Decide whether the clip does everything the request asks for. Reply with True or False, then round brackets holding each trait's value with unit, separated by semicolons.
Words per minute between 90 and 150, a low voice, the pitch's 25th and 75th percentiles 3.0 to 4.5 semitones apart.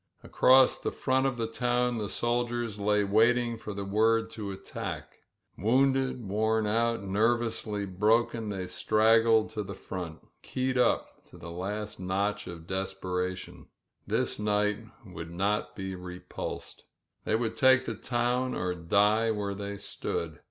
True (145 wpm; 105 Hz; 3.3 semitones)